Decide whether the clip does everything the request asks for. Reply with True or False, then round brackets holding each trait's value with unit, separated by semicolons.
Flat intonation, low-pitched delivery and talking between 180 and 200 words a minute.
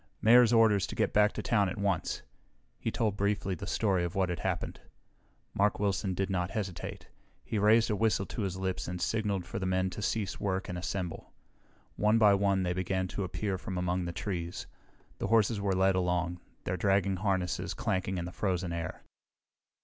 True (2.3 semitones; 95 Hz; 195 wpm)